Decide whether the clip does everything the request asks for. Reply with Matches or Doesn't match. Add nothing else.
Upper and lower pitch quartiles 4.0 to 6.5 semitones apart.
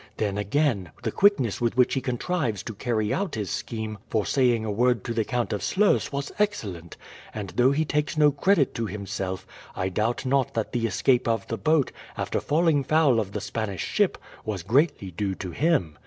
Matches